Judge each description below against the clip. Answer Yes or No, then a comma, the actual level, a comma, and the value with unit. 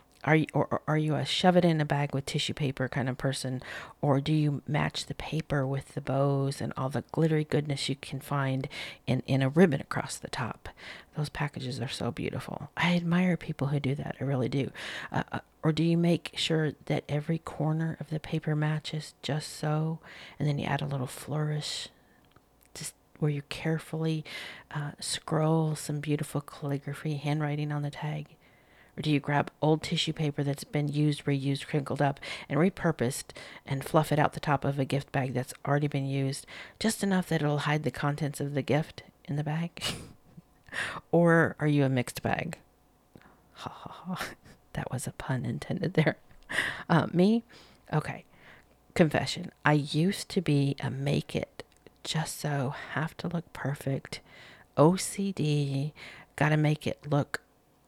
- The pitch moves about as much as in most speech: No, narrow, 2.1 semitones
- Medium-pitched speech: Yes, medium, 145 Hz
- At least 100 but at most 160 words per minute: No, average, 175 wpm